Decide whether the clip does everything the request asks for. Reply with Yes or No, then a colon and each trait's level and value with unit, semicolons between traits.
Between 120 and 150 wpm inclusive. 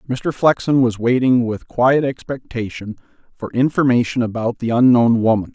Yes: average, 140 wpm